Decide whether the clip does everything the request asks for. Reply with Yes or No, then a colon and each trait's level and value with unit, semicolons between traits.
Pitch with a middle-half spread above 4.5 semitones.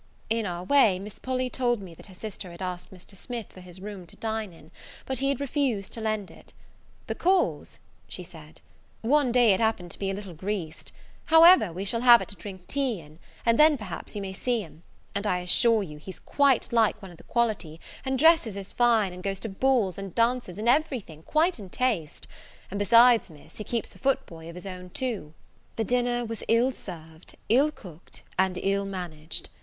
Yes: average, 5.0 semitones